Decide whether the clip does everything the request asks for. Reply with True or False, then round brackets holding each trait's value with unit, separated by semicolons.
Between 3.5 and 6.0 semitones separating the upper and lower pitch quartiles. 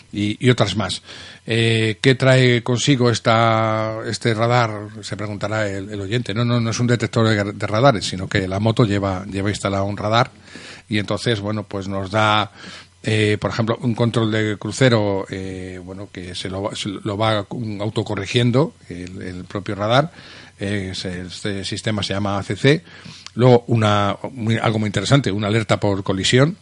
False (2.7 semitones)